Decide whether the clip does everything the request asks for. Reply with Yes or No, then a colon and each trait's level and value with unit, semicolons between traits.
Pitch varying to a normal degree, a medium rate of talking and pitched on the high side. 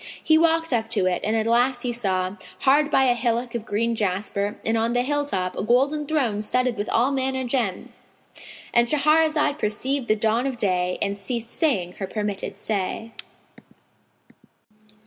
Yes: average, 4.3 semitones; average, 165 wpm; high, 235 Hz